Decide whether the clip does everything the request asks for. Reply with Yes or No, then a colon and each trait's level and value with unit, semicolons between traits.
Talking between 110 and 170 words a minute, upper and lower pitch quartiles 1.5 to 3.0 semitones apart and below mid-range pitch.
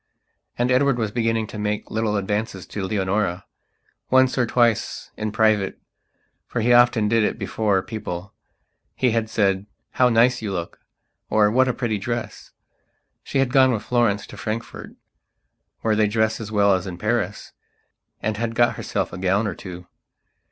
Yes: average, 160 wpm; average, 2.7 semitones; low, 110 Hz